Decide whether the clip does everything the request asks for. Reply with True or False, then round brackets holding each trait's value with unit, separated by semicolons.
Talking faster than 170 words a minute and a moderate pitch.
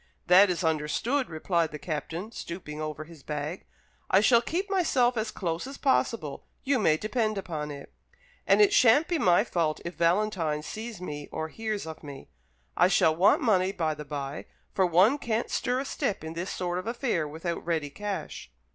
True (185 wpm; 180 Hz)